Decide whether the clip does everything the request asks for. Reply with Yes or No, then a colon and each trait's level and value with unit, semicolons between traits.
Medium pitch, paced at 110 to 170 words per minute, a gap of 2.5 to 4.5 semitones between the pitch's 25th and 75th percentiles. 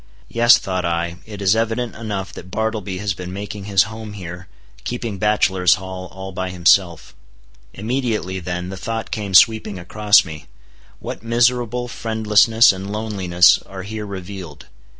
No: low, 100 Hz; average, 150 wpm; average, 3.1 semitones